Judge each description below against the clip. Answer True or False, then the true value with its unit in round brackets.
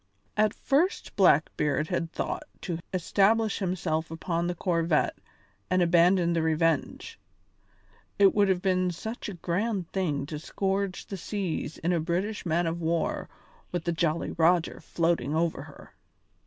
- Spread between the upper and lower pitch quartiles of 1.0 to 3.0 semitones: True (2.7 semitones)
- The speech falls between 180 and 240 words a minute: False (145 wpm)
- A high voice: False (175 Hz)